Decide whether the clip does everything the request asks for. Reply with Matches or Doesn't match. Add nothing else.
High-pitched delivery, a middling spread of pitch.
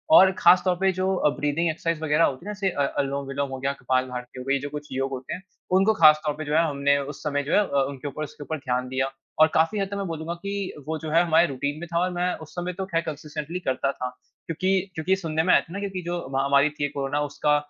Doesn't match